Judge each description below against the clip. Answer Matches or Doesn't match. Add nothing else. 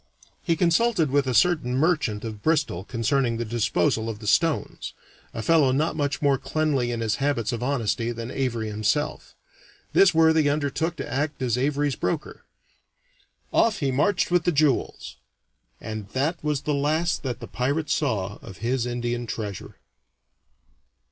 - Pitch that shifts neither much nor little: Matches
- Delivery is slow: Doesn't match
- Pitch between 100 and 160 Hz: Matches